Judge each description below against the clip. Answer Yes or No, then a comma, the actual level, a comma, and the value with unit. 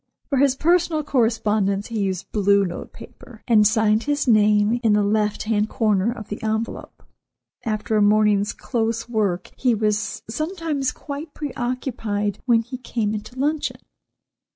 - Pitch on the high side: Yes, high, 220 Hz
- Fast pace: No, average, 155 wpm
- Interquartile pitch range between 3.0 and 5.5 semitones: Yes, average, 3.4 semitones